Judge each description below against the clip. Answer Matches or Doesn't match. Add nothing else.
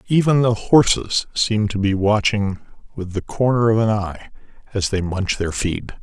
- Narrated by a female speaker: Doesn't match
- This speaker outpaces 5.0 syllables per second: Doesn't match